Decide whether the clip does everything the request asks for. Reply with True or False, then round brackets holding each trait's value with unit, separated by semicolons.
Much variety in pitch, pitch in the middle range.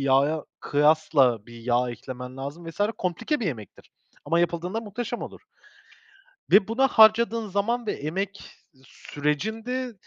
True (7.9 semitones; 170 Hz)